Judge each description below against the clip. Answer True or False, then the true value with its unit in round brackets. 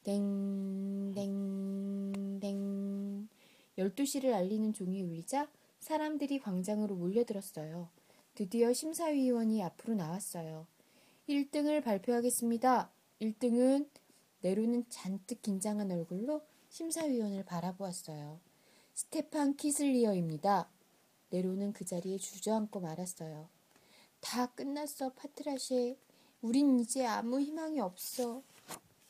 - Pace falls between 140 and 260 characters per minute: True (245 characters per minute)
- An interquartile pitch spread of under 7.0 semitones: True (5.3 semitones)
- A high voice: True (215 Hz)